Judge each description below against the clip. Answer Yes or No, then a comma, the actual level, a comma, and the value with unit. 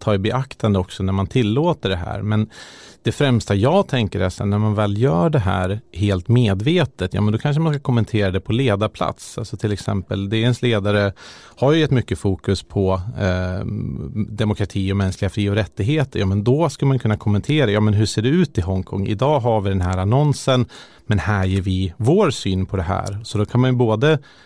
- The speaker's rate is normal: No, fast, 215 wpm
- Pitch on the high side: No, low, 105 Hz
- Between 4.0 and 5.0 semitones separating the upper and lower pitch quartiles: Yes, average, 4.4 semitones